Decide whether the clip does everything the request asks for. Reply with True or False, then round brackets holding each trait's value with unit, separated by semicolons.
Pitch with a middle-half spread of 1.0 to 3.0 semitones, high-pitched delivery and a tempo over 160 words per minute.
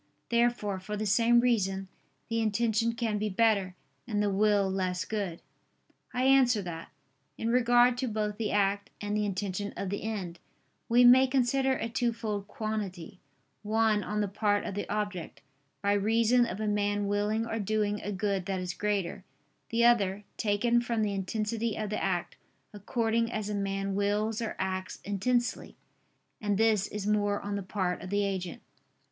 True (2.4 semitones; 210 Hz; 170 wpm)